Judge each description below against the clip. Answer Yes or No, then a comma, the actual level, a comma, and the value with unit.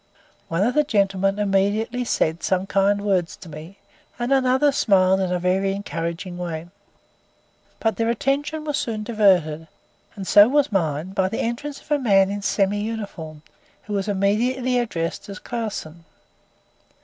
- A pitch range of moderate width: Yes, average, 4.1 semitones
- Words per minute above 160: No, average, 155 wpm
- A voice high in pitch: Yes, high, 200 Hz